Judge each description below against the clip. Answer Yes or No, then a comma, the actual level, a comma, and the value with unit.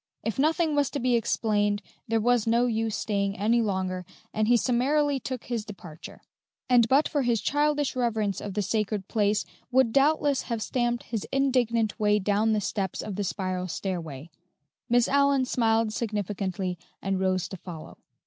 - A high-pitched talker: Yes, high, 220 Hz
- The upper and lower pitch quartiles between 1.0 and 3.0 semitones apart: No, average, 3.8 semitones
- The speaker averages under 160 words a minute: No, average, 165 wpm